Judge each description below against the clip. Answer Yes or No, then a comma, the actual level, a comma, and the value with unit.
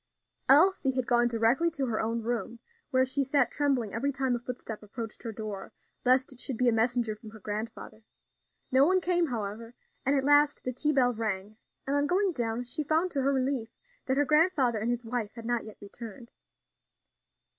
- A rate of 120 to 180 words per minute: No, average, 200 wpm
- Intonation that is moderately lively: Yes, average, 3.5 semitones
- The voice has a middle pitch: No, high, 245 Hz